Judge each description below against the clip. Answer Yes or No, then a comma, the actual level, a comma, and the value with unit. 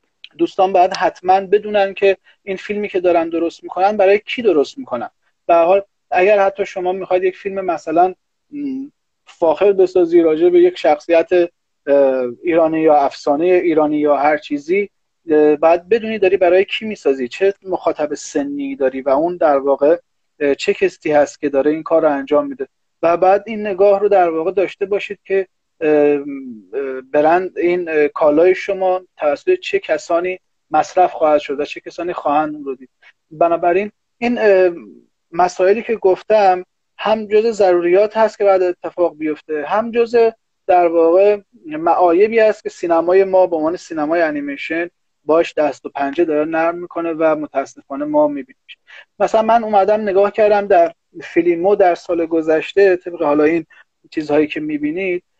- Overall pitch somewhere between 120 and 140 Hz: No, medium, 180 Hz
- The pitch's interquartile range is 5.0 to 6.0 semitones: No, average, 4.3 semitones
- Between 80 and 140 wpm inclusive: No, average, 150 wpm